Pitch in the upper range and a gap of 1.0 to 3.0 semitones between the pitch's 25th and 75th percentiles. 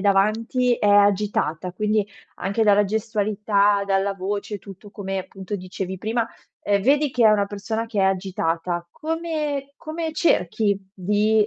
Yes: high, 205 Hz; narrow, 2.5 semitones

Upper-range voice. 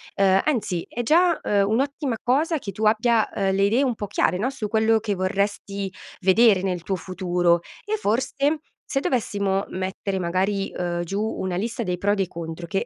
Yes: high, 200 Hz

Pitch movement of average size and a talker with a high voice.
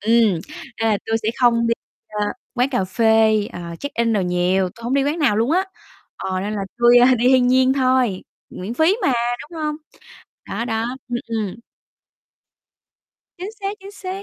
Yes: average, 4.0 semitones; high, 235 Hz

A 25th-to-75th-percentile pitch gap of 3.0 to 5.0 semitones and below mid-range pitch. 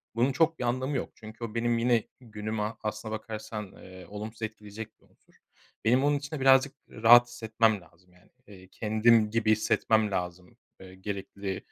No: narrow, 2.4 semitones; low, 110 Hz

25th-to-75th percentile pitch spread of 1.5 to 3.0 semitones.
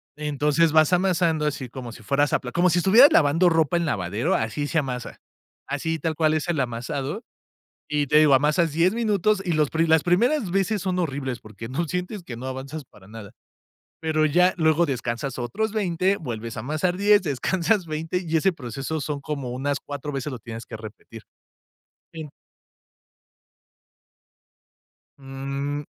No: average, 4.6 semitones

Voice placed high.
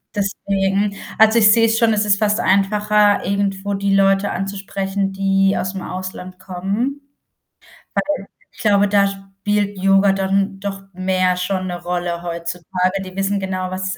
Yes: high, 195 Hz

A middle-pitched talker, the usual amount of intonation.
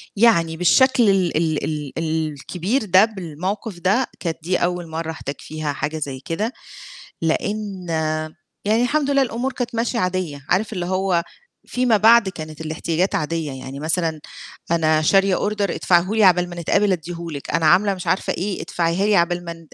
Yes: medium, 180 Hz; average, 4.3 semitones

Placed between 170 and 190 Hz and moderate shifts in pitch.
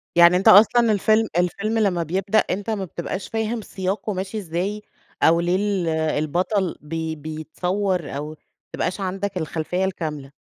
Yes: medium, 185 Hz; average, 3.7 semitones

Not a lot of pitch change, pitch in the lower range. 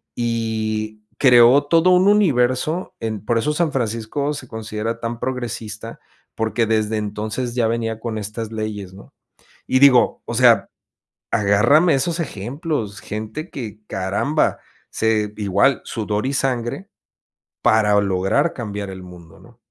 No: average, 3.6 semitones; low, 115 Hz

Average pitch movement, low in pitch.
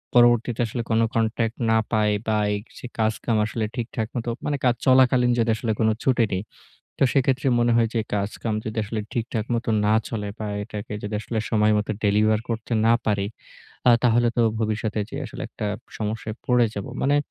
No: narrow, 1.9 semitones; low, 115 Hz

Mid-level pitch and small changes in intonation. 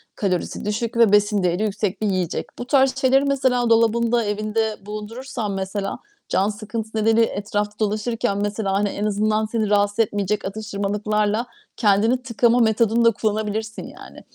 No: high, 215 Hz; narrow, 2.1 semitones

